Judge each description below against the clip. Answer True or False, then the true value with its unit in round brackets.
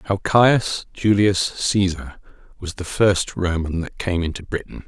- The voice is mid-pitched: False (95 Hz)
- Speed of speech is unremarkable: True (150 wpm)